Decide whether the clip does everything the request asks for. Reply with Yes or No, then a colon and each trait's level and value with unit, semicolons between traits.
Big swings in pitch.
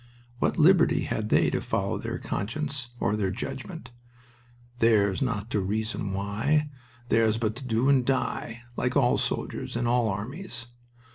No: average, 3.9 semitones